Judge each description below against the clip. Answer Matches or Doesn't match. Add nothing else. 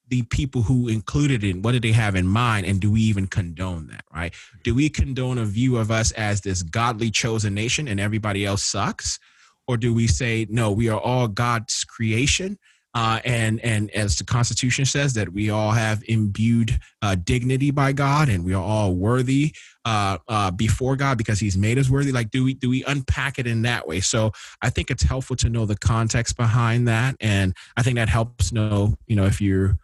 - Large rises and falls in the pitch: Doesn't match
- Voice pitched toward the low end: Matches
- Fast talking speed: Matches